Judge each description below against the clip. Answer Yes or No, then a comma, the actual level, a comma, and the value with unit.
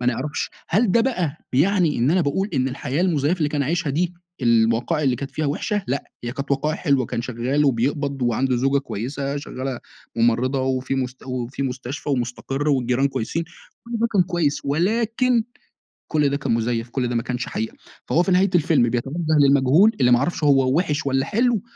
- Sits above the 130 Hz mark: Yes, medium, 140 Hz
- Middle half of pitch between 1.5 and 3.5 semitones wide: No, average, 4.5 semitones